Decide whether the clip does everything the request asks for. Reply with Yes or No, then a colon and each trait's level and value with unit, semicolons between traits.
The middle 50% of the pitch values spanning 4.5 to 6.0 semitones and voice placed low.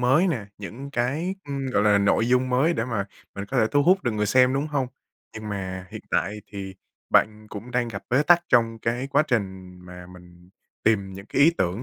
Yes: average, 5.0 semitones; low, 115 Hz